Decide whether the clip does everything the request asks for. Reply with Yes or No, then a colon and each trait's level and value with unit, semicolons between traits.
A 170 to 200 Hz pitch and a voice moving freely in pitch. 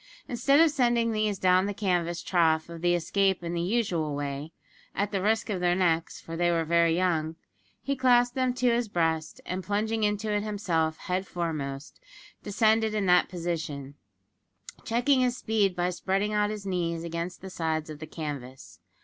No: medium, 185 Hz; average, 4.5 semitones